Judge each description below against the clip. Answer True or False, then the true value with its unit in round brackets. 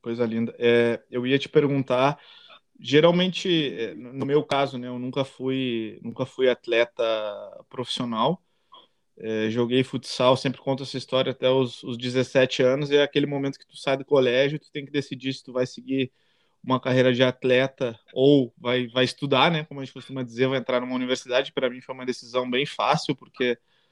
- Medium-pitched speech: False (130 Hz)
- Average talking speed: False (190 wpm)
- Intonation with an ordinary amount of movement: False (1.6 semitones)